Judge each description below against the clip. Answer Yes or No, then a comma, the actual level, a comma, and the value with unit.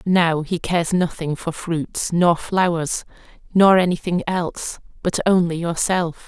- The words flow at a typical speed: Yes, average, 145 wpm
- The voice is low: No, medium, 170 Hz